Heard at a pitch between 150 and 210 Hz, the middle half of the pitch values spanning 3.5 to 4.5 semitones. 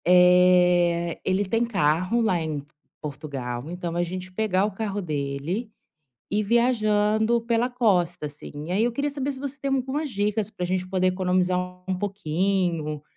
Yes: medium, 185 Hz; average, 4.2 semitones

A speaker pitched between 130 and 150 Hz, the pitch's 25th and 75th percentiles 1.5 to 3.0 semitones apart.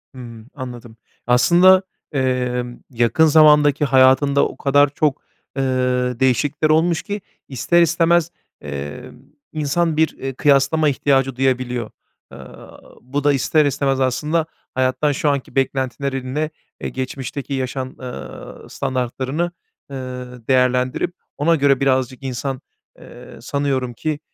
Yes: low, 135 Hz; average, 2.7 semitones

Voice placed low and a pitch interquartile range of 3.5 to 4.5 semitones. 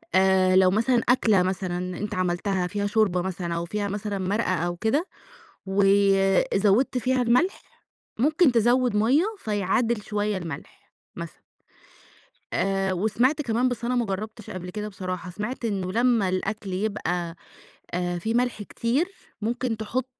No: high, 205 Hz; average, 4.0 semitones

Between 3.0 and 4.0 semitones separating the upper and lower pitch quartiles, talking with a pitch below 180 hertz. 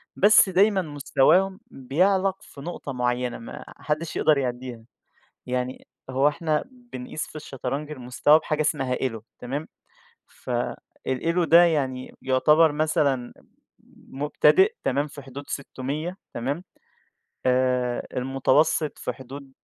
Yes: average, 3.7 semitones; medium, 140 Hz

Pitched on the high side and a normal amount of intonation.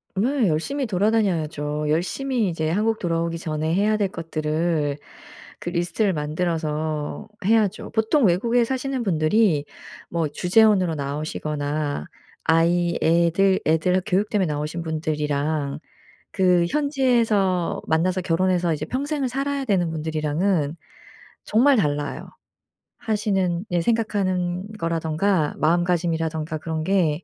No: medium, 175 Hz; average, 4.9 semitones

